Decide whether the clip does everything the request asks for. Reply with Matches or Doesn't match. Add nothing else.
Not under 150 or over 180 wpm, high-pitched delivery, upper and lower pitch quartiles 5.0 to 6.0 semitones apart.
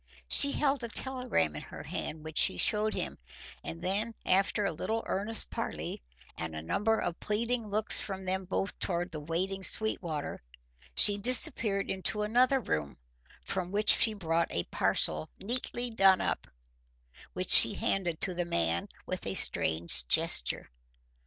Matches